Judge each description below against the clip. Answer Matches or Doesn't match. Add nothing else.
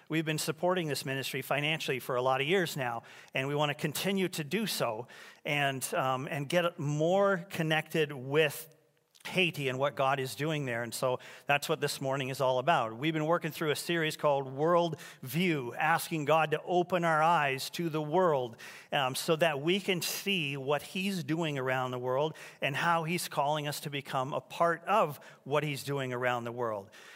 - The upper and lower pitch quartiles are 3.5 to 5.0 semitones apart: Matches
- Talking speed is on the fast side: Doesn't match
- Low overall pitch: Doesn't match